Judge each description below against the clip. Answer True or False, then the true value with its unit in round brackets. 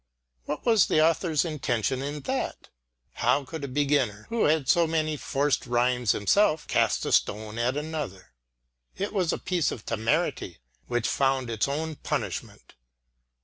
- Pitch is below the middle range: False (145 Hz)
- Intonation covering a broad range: False (4.7 semitones)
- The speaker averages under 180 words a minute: True (150 wpm)